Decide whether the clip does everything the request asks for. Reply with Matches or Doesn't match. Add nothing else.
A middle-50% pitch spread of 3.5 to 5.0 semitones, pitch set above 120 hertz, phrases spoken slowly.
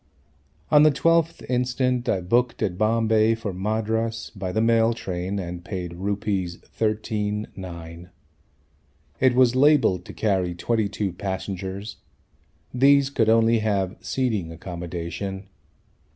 Doesn't match